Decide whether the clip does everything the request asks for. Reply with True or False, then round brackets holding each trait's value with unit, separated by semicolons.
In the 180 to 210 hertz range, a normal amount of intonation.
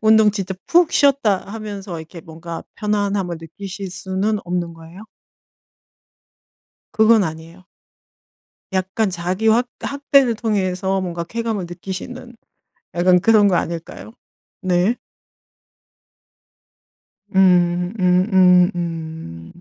True (190 Hz; 3.5 semitones)